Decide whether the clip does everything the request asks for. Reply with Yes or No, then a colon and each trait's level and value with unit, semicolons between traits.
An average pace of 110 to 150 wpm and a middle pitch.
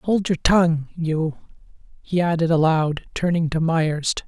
Yes: average, 140 wpm; medium, 165 Hz